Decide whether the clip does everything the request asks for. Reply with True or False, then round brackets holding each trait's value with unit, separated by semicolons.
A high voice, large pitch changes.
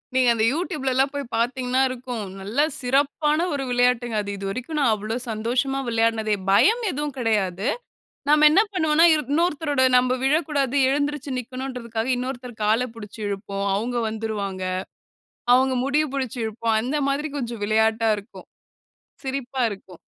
False (250 Hz; 4.1 semitones)